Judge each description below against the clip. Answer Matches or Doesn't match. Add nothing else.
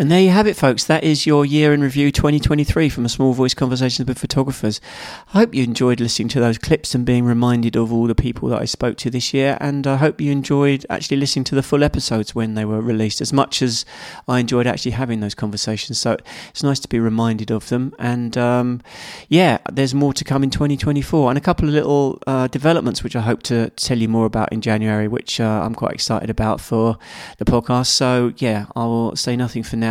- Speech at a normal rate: Doesn't match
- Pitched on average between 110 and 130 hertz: Matches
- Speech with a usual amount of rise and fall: Matches